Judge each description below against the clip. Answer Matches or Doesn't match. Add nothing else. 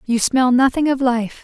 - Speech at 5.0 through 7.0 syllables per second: Doesn't match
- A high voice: Matches